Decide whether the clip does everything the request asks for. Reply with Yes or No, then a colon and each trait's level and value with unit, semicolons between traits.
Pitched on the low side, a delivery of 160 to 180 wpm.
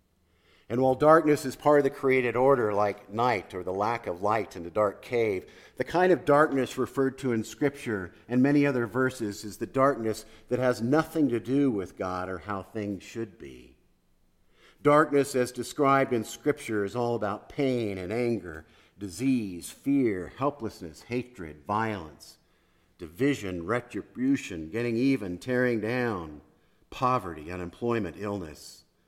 No: low, 120 Hz; average, 150 wpm